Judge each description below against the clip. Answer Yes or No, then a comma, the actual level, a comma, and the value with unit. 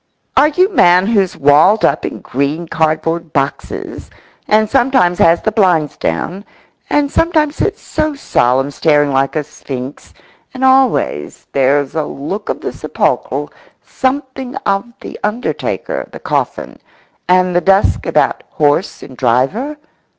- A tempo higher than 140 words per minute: No, slow, 135 wpm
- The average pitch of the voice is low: No, medium, 180 Hz